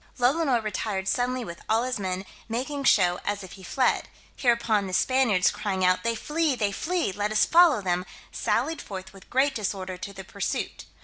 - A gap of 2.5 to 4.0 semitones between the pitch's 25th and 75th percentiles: No, average, 5.1 semitones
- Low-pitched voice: No, high, 215 Hz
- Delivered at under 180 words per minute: No, average, 185 wpm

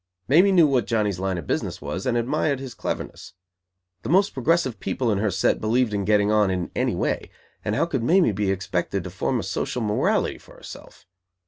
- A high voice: No, low, 110 Hz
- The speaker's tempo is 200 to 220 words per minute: Yes, fast, 205 wpm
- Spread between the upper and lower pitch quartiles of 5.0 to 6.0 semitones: Yes, wide, 5.4 semitones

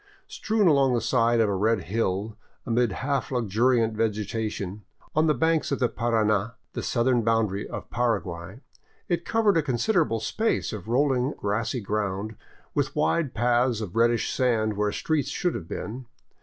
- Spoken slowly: No, average, 155 wpm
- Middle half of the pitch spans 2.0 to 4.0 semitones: Yes, average, 3.6 semitones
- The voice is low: Yes, low, 115 Hz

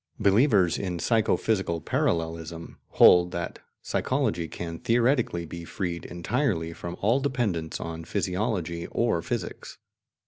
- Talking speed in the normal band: No, slow, 115 wpm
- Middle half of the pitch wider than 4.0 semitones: Yes, average, 4.8 semitones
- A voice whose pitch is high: No, very low, 90 Hz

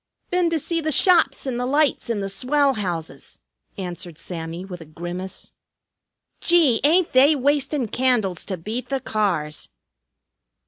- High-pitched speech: Yes, high, 245 Hz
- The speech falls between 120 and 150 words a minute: Yes, average, 145 wpm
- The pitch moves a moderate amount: No, wide, 8.1 semitones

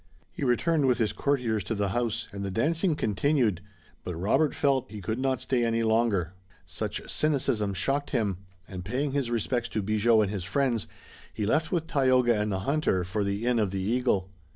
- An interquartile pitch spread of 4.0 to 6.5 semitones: Yes, average, 4.8 semitones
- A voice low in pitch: Yes, low, 115 Hz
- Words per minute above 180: Yes, average, 200 wpm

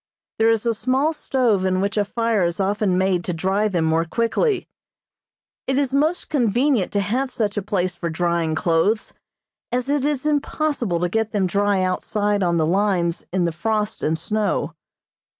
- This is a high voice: Yes, high, 205 Hz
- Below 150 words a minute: No, average, 180 wpm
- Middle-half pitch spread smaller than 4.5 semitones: No, average, 4.9 semitones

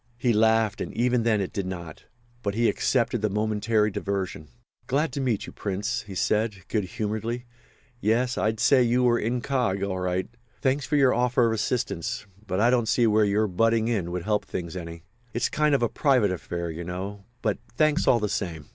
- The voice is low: Yes, low, 110 Hz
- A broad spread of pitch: No, average, 3.8 semitones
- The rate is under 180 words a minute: No, average, 190 wpm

